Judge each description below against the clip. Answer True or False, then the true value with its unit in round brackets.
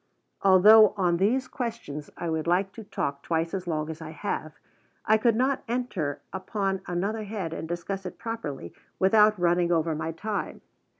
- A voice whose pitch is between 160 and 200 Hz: True (185 Hz)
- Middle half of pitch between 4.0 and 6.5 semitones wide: True (4.8 semitones)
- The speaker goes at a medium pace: True (170 wpm)